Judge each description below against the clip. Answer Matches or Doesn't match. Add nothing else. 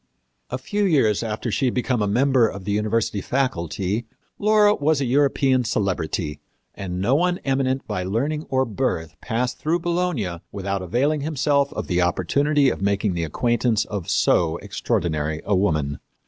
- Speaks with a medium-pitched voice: Doesn't match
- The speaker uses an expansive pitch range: Matches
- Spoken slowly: Doesn't match